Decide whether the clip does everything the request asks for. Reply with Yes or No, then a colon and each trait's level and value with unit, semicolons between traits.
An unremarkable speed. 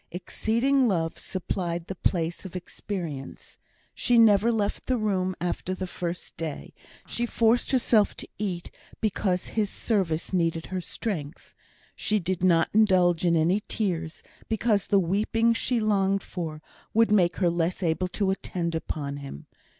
Yes: average, 150 wpm